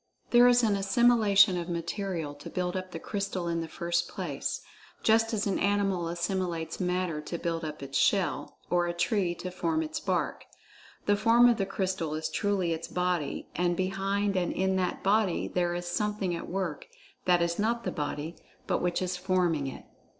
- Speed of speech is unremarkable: Yes, average, 185 wpm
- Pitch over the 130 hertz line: Yes, medium, 185 Hz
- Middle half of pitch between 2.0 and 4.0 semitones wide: Yes, average, 2.9 semitones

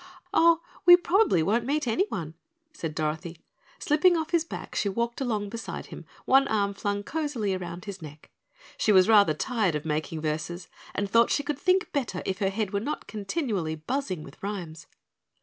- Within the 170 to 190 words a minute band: Yes, average, 180 wpm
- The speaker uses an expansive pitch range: Yes, wide, 8.2 semitones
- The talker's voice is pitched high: Yes, high, 205 Hz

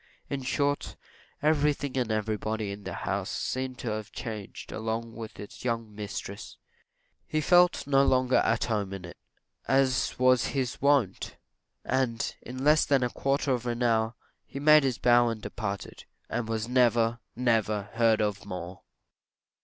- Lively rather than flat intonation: No, average, 3.4 semitones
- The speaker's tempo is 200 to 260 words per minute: No, average, 155 wpm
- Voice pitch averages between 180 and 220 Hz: No, low, 120 Hz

